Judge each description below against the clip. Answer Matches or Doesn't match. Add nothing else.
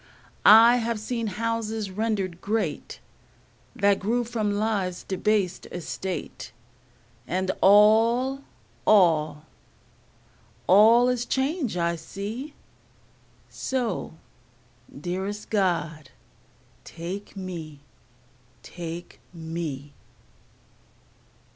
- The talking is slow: Matches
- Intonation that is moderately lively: Matches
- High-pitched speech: Matches